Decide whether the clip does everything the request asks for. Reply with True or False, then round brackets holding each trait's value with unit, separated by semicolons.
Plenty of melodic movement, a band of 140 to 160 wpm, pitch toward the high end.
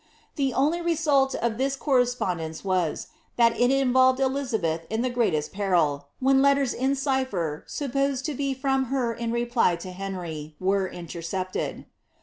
True (6.6 semitones; 150 wpm; 240 Hz)